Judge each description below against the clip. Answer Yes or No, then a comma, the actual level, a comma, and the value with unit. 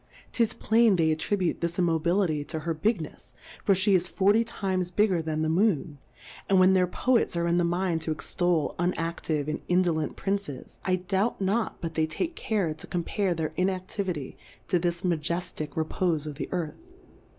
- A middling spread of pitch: Yes, average, 3.2 semitones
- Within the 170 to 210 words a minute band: Yes, average, 175 wpm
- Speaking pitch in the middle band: Yes, medium, 175 Hz